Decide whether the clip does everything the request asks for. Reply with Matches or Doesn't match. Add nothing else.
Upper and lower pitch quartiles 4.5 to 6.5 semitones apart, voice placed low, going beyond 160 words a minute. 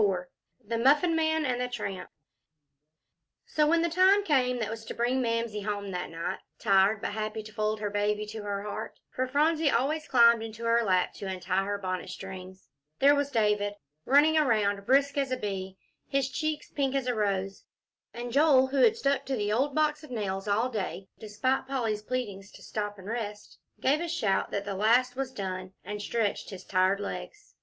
Doesn't match